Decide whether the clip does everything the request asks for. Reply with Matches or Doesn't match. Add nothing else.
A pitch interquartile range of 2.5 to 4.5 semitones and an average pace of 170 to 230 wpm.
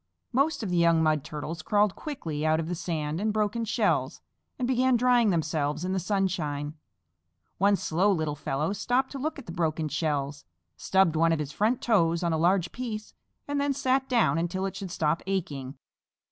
Doesn't match